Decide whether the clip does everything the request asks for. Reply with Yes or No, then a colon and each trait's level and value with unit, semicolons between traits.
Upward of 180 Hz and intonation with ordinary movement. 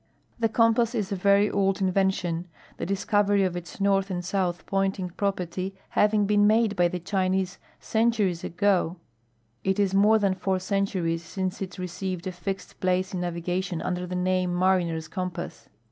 No: high, 190 Hz; narrow, 1.9 semitones